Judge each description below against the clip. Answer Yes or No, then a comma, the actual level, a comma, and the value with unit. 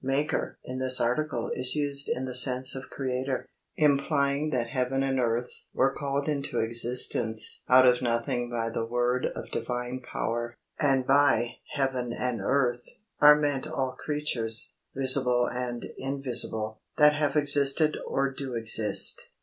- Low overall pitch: Yes, low, 130 Hz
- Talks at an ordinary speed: Yes, average, 145 wpm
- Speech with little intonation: Yes, narrow, 2.3 semitones